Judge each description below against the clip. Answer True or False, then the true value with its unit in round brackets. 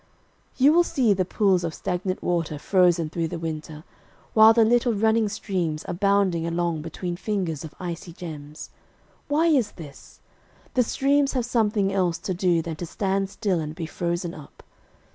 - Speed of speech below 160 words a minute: False (170 wpm)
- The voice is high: False (180 Hz)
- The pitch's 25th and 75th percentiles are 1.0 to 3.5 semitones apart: False (4.5 semitones)